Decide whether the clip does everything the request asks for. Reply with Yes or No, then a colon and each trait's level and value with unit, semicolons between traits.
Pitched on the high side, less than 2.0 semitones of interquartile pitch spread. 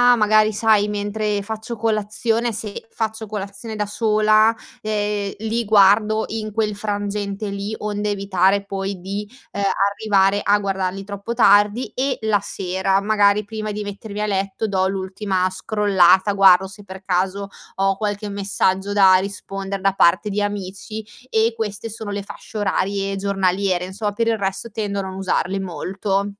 Yes: high, 205 Hz; narrow, 1.6 semitones